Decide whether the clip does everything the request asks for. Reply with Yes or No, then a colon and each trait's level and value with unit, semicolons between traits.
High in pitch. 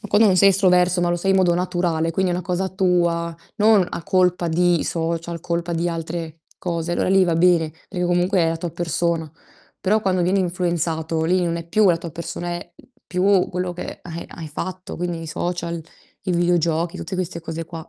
No: medium, 175 Hz